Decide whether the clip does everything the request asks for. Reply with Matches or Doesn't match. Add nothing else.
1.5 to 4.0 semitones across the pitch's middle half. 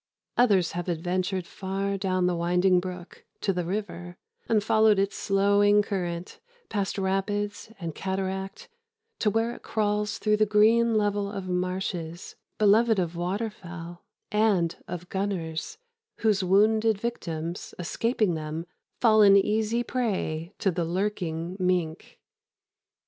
Matches